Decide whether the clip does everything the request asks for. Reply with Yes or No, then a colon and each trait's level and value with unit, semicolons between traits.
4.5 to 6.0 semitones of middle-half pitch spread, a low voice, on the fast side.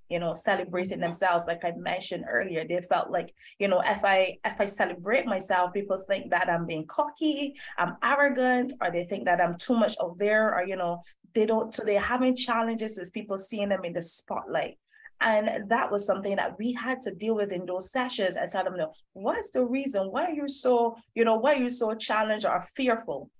No: average, 5.1 semitones; high, 210 Hz; fast, 220 wpm